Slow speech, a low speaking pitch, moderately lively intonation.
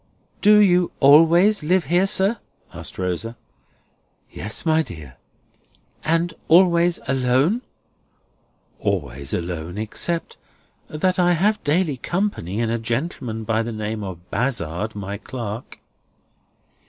No: slow, 115 wpm; low, 130 Hz; wide, 8.7 semitones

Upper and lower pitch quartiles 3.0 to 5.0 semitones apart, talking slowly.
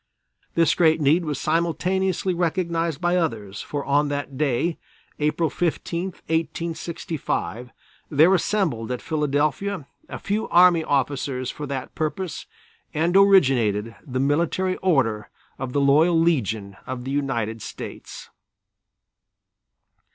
Yes: average, 4.4 semitones; slow, 115 wpm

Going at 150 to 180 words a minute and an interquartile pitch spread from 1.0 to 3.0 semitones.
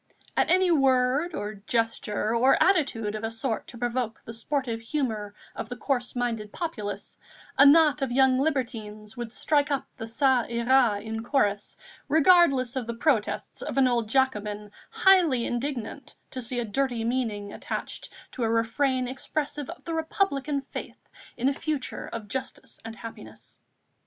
No: average, 160 wpm; average, 3.6 semitones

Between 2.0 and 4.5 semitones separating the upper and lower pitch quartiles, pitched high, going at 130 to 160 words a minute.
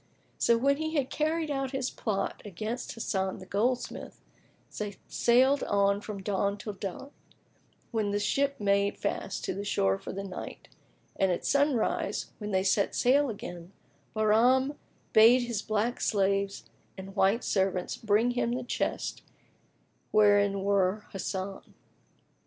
Yes: average, 3.8 semitones; high, 210 Hz; average, 140 wpm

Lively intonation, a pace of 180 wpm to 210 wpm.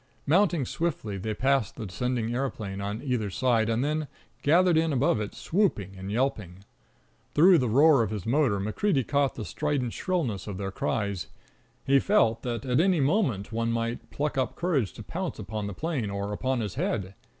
Yes: wide, 6.0 semitones; average, 185 wpm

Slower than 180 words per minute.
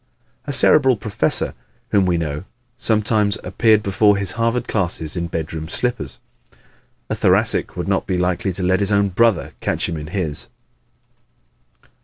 Yes: average, 150 wpm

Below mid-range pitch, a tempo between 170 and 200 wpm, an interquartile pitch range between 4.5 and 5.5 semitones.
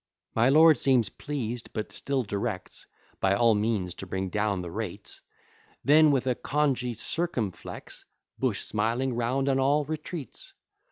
No: low, 120 Hz; average, 145 wpm; average, 4.8 semitones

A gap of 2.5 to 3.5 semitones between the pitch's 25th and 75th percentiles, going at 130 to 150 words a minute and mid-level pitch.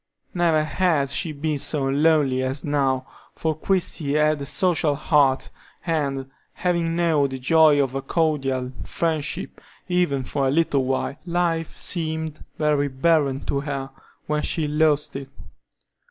Yes: average, 3.0 semitones; average, 140 wpm; medium, 150 Hz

